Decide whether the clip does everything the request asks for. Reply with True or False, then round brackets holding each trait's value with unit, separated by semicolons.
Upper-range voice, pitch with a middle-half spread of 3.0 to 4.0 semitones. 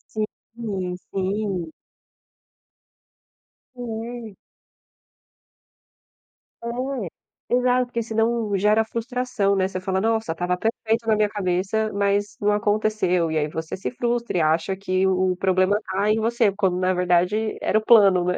True (205 Hz; 3.3 semitones)